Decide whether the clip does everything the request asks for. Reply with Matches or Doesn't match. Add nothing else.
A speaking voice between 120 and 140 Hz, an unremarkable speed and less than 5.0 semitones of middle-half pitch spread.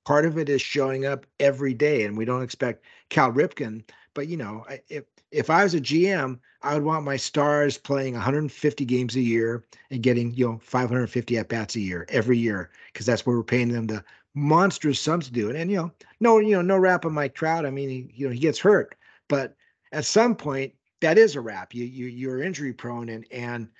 Doesn't match